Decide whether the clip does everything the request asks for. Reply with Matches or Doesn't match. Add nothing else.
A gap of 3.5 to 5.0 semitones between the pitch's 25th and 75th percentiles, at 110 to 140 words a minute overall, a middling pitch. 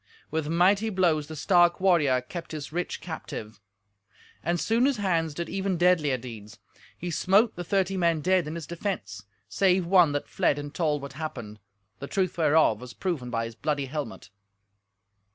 Doesn't match